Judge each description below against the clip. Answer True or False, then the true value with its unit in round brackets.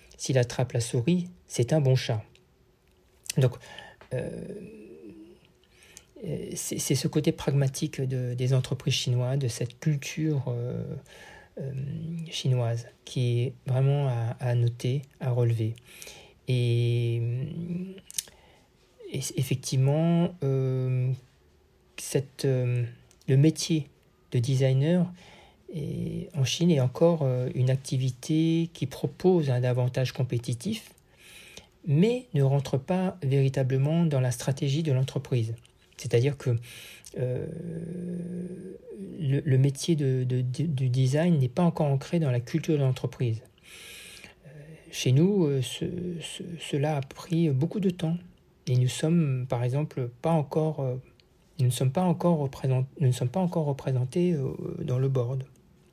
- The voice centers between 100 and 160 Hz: True (140 Hz)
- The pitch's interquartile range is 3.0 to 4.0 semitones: False (4.4 semitones)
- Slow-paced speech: True (120 wpm)